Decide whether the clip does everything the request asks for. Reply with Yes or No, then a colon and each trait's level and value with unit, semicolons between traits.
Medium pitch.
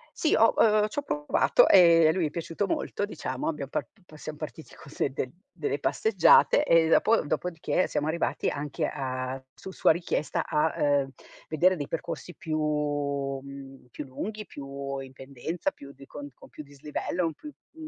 Yes: medium, 150 Hz